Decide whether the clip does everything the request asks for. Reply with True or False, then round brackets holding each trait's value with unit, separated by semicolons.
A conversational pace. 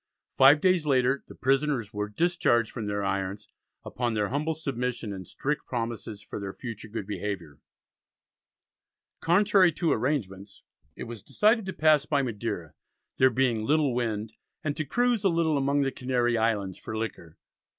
True (160 wpm)